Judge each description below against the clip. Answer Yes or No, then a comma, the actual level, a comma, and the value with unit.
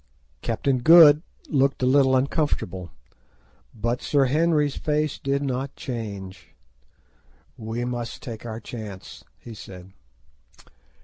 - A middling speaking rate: No, slow, 110 wpm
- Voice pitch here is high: No, low, 125 Hz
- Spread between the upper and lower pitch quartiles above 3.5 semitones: Yes, average, 4.3 semitones